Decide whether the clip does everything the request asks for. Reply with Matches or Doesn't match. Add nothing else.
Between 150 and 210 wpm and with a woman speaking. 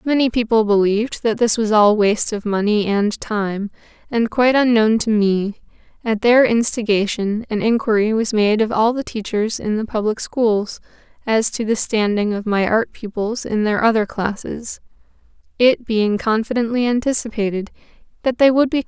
Matches